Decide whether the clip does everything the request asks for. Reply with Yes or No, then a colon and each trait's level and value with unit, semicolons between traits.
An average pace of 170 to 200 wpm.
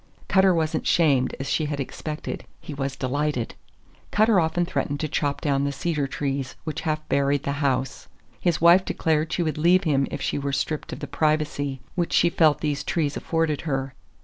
Yes: average, 195 wpm